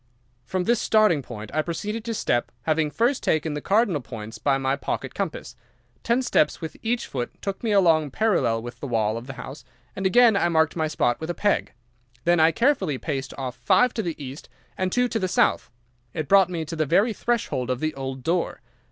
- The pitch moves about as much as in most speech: No, wide, 7.3 semitones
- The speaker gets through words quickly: Yes, fast, 215 wpm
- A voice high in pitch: No, medium, 160 Hz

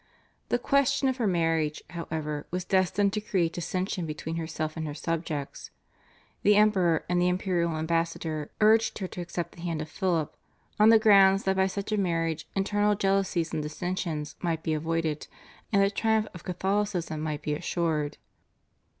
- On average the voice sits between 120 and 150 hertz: No, medium, 175 Hz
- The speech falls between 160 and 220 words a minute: Yes, average, 165 wpm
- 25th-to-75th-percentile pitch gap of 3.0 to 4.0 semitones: Yes, average, 3.6 semitones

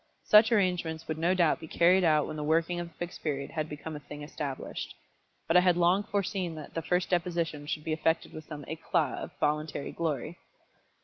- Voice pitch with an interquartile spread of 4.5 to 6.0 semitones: No, narrow, 2.6 semitones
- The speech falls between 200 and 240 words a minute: Yes, fast, 205 wpm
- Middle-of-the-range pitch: Yes, medium, 165 Hz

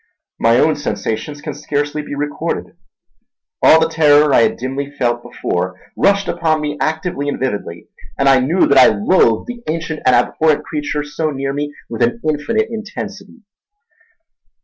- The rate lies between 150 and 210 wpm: Yes, average, 160 wpm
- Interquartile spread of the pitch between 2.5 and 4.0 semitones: Yes, average, 3.4 semitones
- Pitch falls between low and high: Yes, medium, 145 Hz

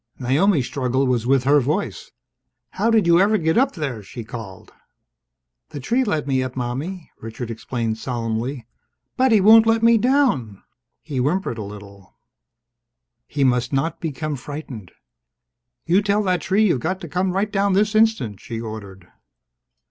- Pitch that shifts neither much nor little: No, wide, 8.5 semitones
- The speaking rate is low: No, average, 160 wpm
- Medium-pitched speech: Yes, medium, 145 Hz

